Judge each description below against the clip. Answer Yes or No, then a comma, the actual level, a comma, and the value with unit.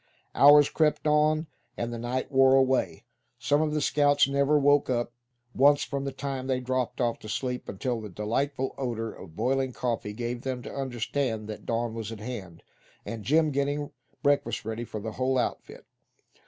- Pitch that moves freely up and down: No, average, 3.3 semitones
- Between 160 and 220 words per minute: Yes, average, 180 wpm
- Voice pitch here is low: Yes, low, 130 Hz